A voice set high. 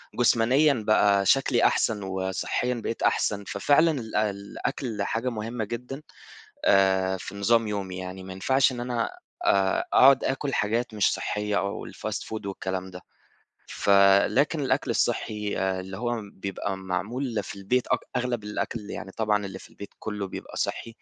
No: low, 105 Hz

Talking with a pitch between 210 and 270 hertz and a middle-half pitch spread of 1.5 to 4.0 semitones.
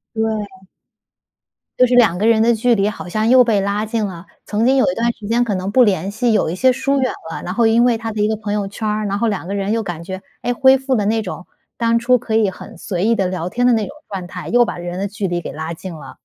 Yes: high, 215 Hz; average, 3.6 semitones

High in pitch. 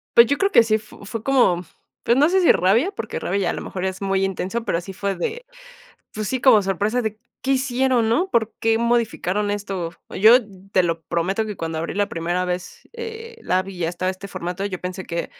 Yes: high, 205 Hz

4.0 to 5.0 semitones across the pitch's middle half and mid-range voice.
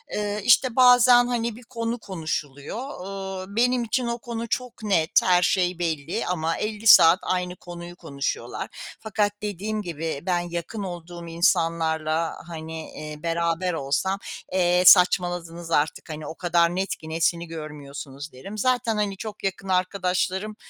Yes: average, 4.3 semitones; medium, 180 Hz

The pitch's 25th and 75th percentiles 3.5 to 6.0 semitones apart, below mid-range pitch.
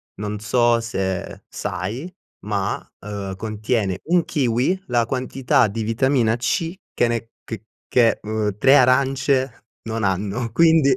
Yes: average, 3.9 semitones; low, 115 Hz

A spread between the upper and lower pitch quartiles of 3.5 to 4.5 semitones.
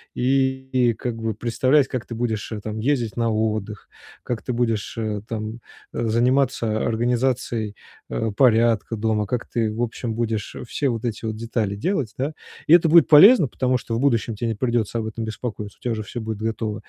No: narrow, 2.4 semitones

